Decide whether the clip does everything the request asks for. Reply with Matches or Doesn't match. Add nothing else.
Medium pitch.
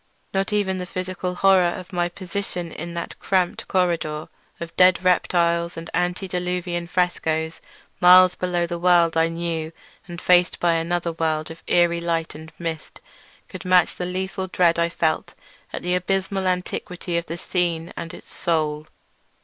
Matches